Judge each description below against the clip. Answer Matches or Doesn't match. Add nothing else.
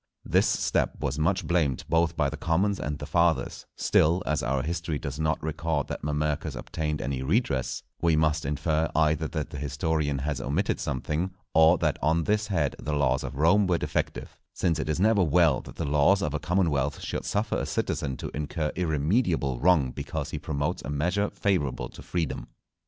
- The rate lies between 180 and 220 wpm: Matches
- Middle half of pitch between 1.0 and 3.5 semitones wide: Matches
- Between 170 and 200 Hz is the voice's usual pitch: Doesn't match